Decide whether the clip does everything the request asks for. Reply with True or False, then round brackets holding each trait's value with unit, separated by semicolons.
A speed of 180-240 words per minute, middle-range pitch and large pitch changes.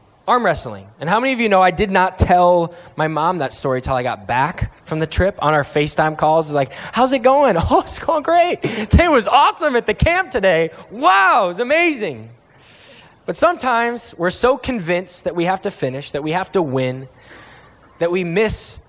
True (205 wpm; 180 Hz; 7.9 semitones)